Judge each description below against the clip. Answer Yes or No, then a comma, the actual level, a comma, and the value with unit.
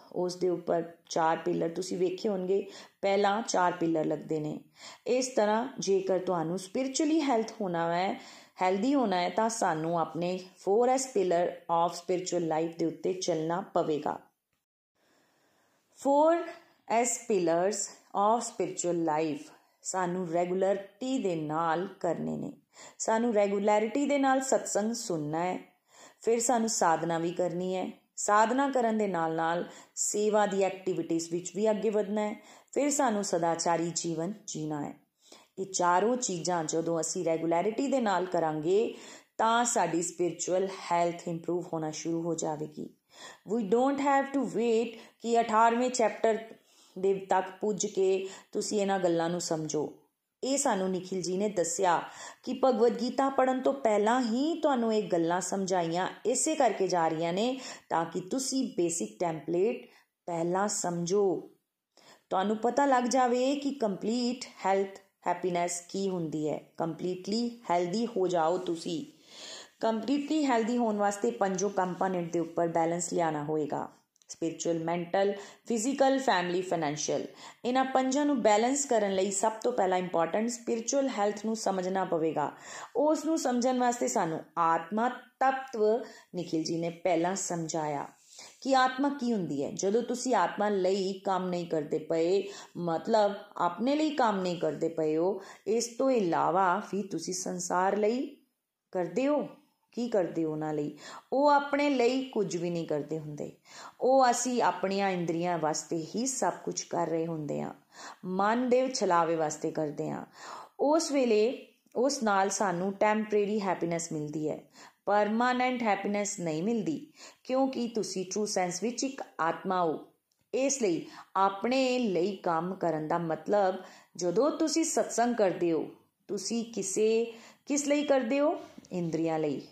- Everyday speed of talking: Yes, average, 140 wpm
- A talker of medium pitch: No, high, 195 Hz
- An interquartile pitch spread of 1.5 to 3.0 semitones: No, wide, 5.5 semitones